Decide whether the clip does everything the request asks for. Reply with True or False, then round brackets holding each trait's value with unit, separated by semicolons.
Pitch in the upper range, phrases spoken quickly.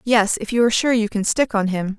True (220 Hz; 305 wpm)